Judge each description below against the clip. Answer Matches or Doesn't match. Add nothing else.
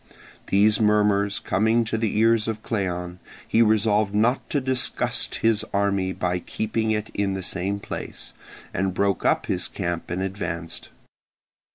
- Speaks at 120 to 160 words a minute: Matches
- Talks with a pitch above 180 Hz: Doesn't match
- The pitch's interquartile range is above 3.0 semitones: Doesn't match